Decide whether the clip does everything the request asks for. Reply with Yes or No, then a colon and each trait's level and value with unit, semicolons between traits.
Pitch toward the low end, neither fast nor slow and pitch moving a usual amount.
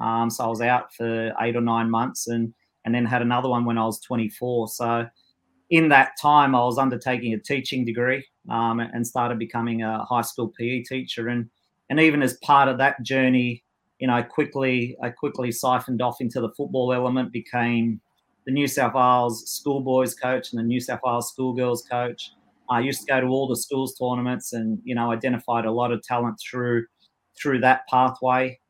No: low, 120 Hz; average, 195 wpm; narrow, 1.8 semitones